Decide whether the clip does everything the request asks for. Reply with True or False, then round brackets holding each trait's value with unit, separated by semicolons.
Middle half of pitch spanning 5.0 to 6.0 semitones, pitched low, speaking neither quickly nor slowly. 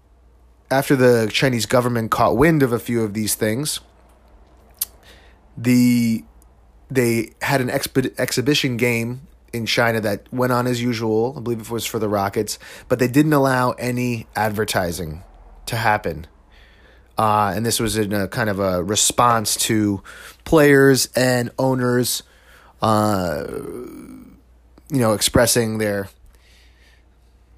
False (5.4 semitones; 110 Hz; 130 wpm)